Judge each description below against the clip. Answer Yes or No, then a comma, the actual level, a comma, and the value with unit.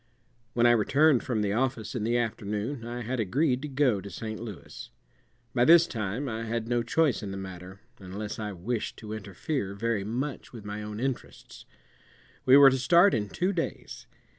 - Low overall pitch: Yes, low, 115 Hz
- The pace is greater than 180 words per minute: Yes, average, 190 wpm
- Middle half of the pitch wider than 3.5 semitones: Yes, average, 4.0 semitones